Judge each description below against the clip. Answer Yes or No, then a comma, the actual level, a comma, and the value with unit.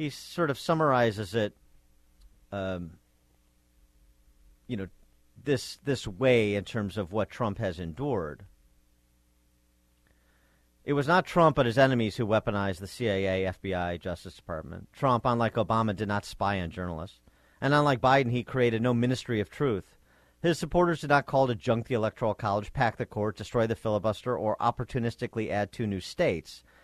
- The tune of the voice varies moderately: No, wide, 6.4 semitones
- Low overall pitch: Yes, low, 105 Hz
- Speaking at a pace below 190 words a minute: Yes, average, 160 wpm